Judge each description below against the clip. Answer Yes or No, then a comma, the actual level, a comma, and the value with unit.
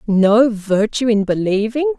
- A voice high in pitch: Yes, high, 225 Hz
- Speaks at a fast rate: No, slow, 120 wpm